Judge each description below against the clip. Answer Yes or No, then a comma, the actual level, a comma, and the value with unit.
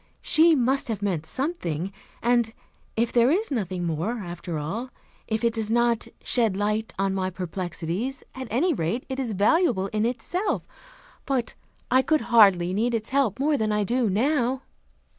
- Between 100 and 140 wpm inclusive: No, average, 165 wpm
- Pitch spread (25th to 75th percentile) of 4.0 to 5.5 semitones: Yes, average, 5.1 semitones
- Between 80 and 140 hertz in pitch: No, high, 225 Hz